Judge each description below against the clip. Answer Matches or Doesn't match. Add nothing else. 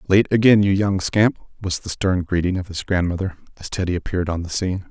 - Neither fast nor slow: Doesn't match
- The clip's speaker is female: Doesn't match